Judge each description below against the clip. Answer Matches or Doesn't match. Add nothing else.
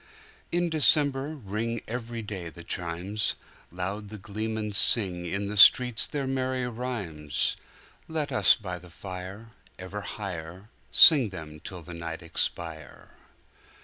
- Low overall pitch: Matches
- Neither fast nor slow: Doesn't match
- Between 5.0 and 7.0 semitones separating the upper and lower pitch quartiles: Matches